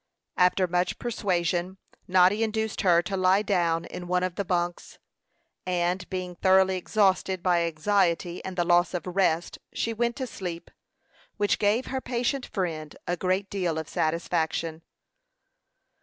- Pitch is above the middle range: No, medium, 180 Hz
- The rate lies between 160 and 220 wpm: No, average, 145 wpm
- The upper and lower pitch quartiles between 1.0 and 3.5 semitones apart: Yes, narrow, 2.4 semitones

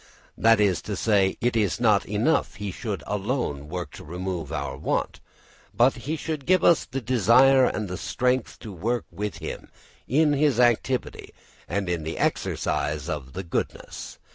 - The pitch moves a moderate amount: No, wide, 5.9 semitones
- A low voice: Yes, low, 105 Hz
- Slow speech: No, average, 165 wpm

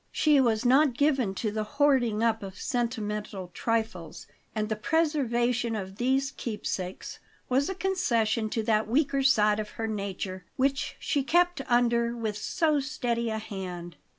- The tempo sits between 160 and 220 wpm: No, average, 150 wpm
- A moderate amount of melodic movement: Yes, average, 4.2 semitones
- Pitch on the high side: Yes, high, 235 Hz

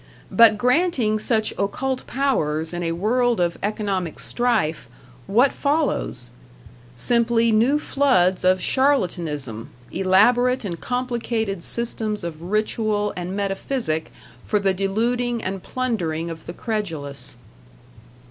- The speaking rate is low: Yes, slow, 110 wpm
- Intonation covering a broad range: Yes, wide, 5.7 semitones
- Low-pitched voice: No, high, 210 Hz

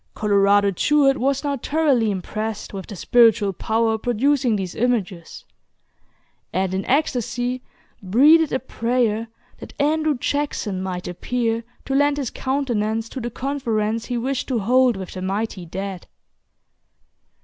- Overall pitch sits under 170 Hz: No, high, 230 Hz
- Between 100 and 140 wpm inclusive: Yes, slow, 135 wpm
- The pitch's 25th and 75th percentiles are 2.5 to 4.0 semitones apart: No, average, 4.8 semitones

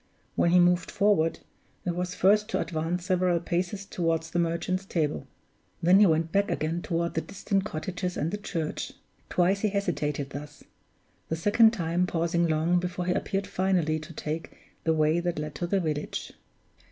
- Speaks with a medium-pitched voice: Yes, medium, 175 Hz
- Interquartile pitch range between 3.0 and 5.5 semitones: No, narrow, 2.4 semitones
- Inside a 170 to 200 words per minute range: Yes, average, 175 wpm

